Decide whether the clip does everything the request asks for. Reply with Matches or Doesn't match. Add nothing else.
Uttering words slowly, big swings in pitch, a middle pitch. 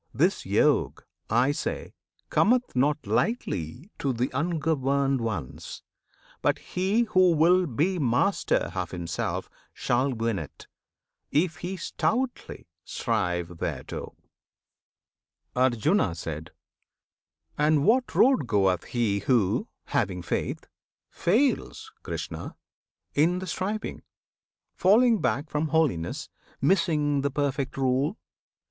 Matches